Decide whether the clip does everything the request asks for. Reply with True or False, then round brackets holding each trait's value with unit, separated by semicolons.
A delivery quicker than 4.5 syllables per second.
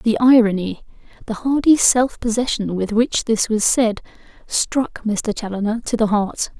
False (4.4 syllables/s)